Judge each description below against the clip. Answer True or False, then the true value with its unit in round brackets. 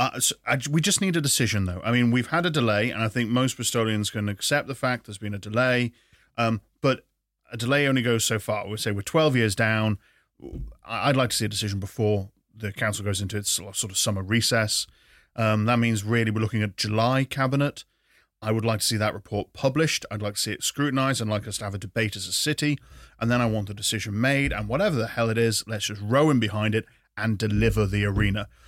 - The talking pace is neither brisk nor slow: False (240 wpm)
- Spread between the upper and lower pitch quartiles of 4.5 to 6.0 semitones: False (3.1 semitones)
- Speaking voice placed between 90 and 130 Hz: True (110 Hz)